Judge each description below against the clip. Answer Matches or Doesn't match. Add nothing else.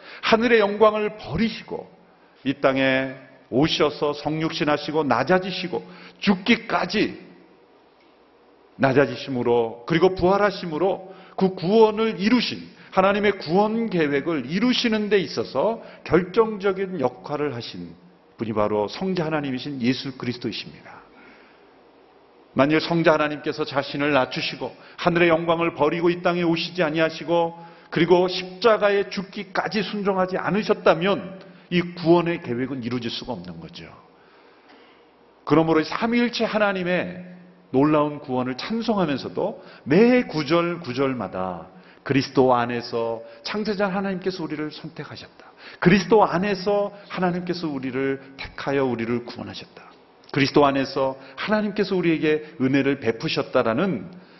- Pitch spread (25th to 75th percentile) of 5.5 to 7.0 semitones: Matches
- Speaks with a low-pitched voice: Doesn't match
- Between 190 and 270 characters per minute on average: Doesn't match